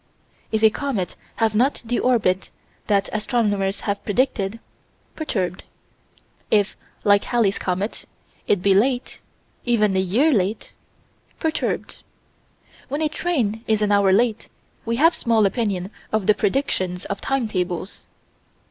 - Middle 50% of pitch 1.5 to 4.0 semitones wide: Yes, average, 3.7 semitones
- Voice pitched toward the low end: No, high, 215 Hz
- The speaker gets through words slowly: Yes, slow, 130 wpm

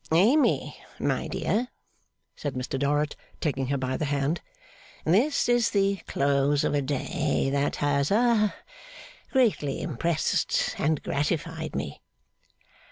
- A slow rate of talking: Yes, slow, 120 wpm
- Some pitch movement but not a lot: No, wide, 5.9 semitones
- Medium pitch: Yes, medium, 150 Hz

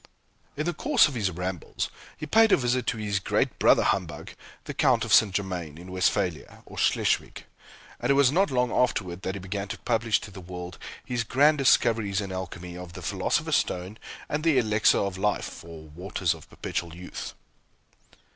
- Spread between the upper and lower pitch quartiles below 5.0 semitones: No, average, 5.3 semitones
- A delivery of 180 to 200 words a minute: Yes, average, 185 wpm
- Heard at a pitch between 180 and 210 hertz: No, low, 100 Hz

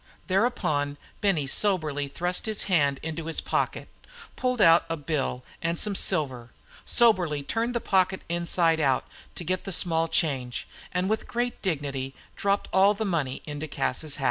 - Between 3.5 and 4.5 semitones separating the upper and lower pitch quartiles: No, average, 5.1 semitones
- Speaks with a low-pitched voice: No, medium, 165 Hz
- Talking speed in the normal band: Yes, average, 160 wpm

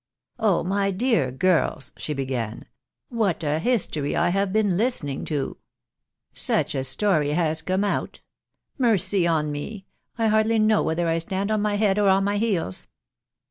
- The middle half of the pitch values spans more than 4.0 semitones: Yes, average, 5.2 semitones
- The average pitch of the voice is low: No, high, 190 Hz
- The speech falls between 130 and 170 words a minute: No, average, 185 wpm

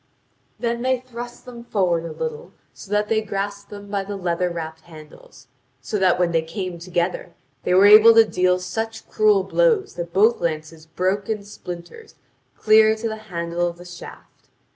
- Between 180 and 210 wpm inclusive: Yes, average, 185 wpm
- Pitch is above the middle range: Yes, high, 200 Hz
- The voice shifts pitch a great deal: No, average, 4.2 semitones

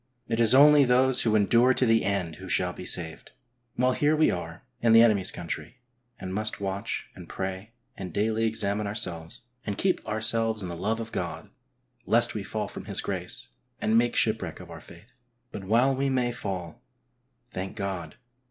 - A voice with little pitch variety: No, average, 4.0 semitones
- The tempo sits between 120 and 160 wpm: No, average, 185 wpm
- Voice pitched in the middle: No, low, 105 Hz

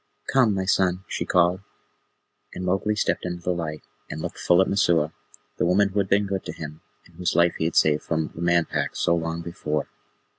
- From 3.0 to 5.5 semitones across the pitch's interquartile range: No, narrow, 2.6 semitones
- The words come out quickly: Yes, fast, 215 wpm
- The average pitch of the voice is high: No, very low, 85 Hz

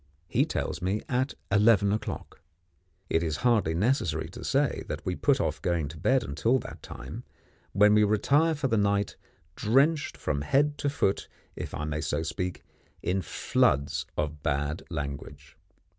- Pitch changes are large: Yes, wide, 7.5 semitones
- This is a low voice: Yes, low, 100 Hz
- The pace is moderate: Yes, average, 160 wpm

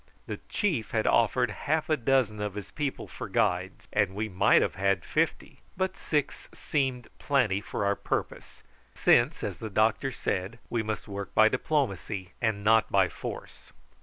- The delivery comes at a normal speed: Yes, average, 165 wpm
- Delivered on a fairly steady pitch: No, average, 4.8 semitones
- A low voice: Yes, low, 110 Hz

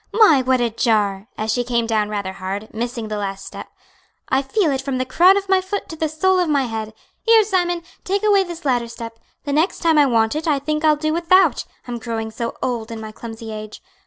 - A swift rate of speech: Yes, fast, 235 wpm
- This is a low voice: No, very high, 255 Hz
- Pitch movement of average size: No, wide, 6.9 semitones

